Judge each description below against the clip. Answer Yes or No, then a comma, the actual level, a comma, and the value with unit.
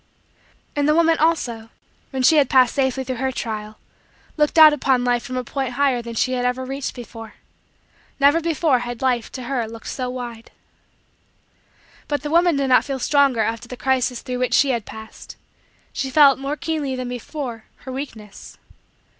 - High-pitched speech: Yes, very high, 255 Hz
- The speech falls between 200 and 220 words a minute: No, average, 180 wpm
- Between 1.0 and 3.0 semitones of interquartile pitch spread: Yes, average, 2.7 semitones